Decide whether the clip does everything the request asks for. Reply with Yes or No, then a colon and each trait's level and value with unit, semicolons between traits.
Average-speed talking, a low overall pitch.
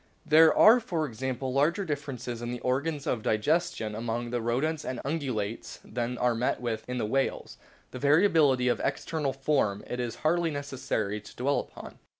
Yes: average, 170 wpm; low, 130 Hz